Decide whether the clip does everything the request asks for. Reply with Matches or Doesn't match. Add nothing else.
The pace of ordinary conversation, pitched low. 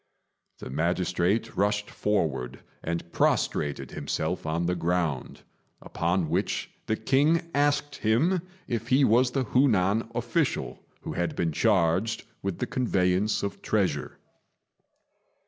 Doesn't match